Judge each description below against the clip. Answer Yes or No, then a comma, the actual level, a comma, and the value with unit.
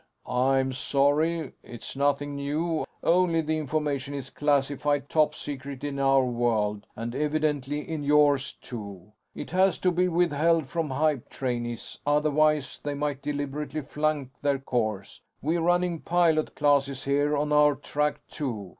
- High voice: No, medium, 145 Hz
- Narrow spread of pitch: Yes, narrow, 2.3 semitones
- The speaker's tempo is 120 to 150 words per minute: Yes, average, 140 wpm